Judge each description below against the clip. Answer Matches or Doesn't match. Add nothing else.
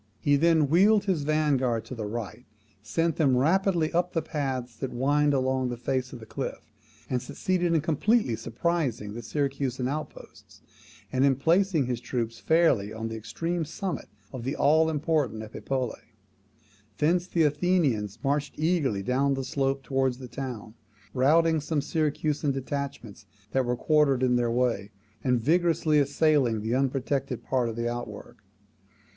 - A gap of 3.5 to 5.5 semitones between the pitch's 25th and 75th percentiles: Matches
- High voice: Doesn't match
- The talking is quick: Doesn't match